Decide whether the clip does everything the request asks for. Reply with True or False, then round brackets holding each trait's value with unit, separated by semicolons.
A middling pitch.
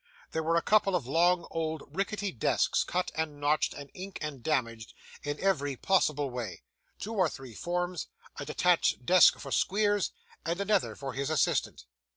True (160 Hz)